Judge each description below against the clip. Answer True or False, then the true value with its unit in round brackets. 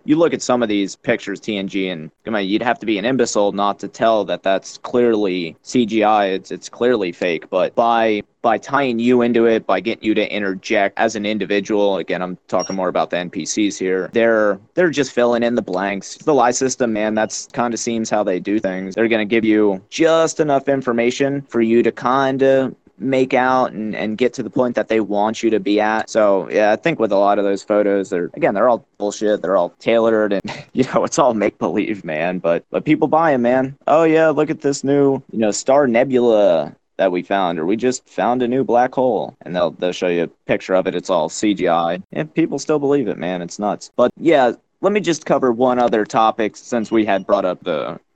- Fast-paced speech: True (230 wpm)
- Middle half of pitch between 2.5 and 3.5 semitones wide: False (4.2 semitones)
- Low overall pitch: True (110 Hz)